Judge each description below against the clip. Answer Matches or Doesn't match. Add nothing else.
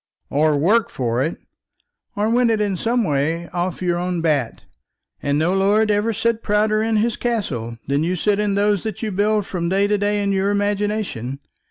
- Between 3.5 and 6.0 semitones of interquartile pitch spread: Matches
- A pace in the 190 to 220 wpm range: Matches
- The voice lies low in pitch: Doesn't match